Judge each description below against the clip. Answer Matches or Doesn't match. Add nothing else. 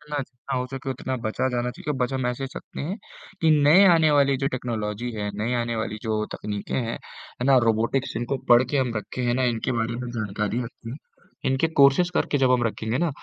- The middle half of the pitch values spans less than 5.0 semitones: Matches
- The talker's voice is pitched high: Doesn't match